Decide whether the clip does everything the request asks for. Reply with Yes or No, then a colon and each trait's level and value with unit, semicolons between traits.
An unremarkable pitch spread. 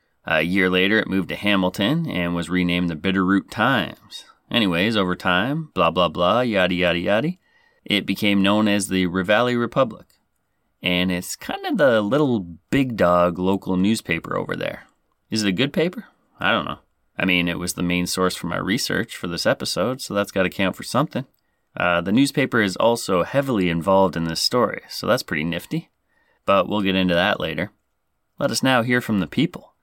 Yes: average, 3.5 semitones